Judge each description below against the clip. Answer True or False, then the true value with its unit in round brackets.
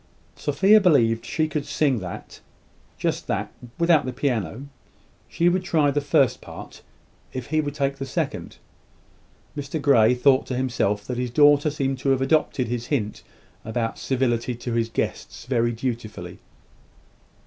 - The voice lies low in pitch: True (130 Hz)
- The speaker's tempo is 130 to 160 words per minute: True (150 wpm)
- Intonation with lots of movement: False (3.6 semitones)